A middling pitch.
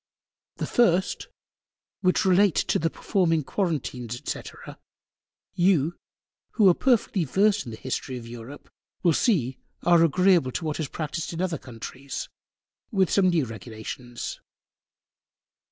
Yes: medium, 165 Hz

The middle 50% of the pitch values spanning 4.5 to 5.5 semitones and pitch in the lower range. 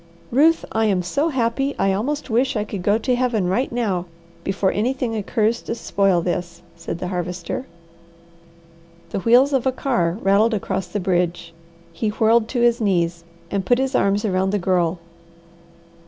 No: average, 4.8 semitones; high, 210 Hz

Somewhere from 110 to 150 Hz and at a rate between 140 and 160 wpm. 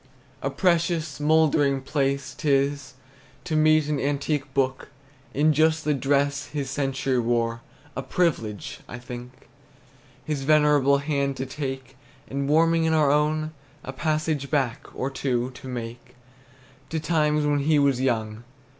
Yes: medium, 140 Hz; average, 145 wpm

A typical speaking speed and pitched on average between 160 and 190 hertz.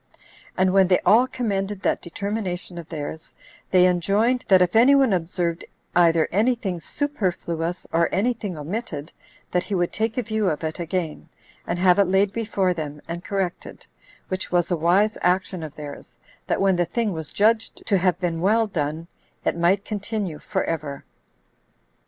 Yes: average, 175 wpm; medium, 185 Hz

